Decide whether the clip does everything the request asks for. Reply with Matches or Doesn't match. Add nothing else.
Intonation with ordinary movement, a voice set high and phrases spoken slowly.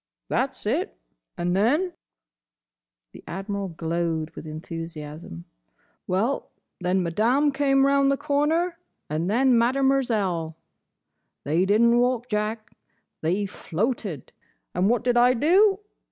Doesn't match